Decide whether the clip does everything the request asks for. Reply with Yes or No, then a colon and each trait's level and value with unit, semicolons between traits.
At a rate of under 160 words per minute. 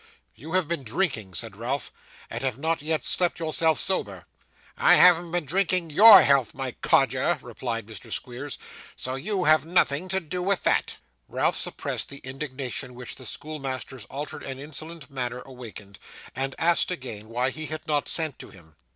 No: average, 170 wpm